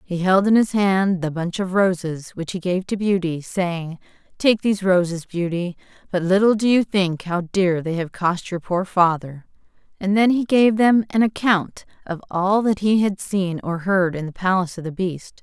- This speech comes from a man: No, female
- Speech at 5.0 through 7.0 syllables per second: No, 4.6 syllables/s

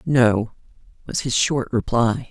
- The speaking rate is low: Yes, slow, 130 wpm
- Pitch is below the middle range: Yes, low, 120 Hz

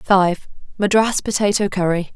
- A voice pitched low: No, high, 195 Hz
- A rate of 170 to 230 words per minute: No, slow, 85 wpm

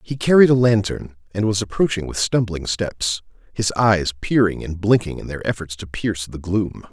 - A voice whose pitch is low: Yes, low, 100 Hz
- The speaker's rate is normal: Yes, average, 190 wpm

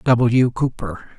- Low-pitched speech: Yes, low, 115 Hz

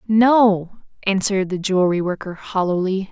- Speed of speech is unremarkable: No, slow, 115 wpm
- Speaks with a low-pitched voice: No, high, 195 Hz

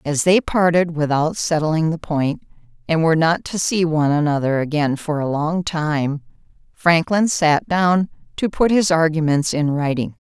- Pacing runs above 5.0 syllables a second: No, 4.5 syllables/s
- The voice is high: No, medium, 160 Hz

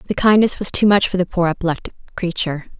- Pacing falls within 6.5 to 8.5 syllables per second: Yes, 7.0 syllables/s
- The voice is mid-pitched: Yes, medium, 180 Hz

